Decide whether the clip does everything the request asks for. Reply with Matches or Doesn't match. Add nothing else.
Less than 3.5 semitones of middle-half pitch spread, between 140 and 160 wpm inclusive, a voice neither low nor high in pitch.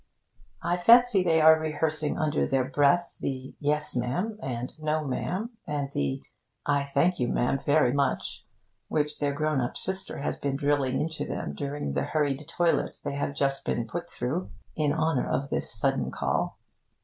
Doesn't match